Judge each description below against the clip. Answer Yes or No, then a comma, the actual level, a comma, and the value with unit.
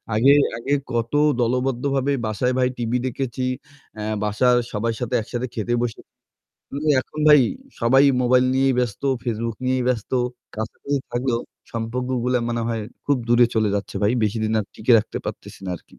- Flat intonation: Yes, narrow, 2.2 semitones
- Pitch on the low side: Yes, low, 120 Hz